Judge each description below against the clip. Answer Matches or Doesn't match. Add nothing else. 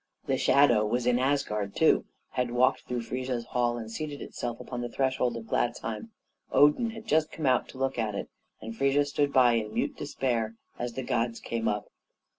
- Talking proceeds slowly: Doesn't match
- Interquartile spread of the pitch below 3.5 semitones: Matches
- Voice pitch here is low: Matches